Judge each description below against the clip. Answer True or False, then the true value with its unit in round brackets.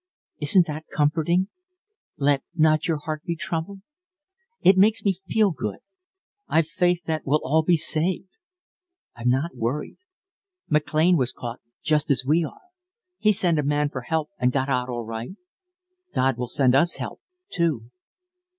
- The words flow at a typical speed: True (155 wpm)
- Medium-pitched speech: True (155 Hz)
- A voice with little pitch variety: False (4.3 semitones)